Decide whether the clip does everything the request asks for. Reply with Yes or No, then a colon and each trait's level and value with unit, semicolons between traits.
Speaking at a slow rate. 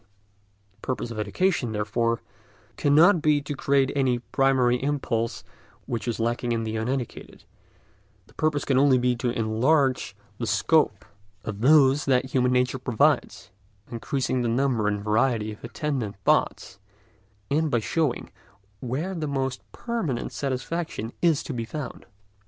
No: average, 145 wpm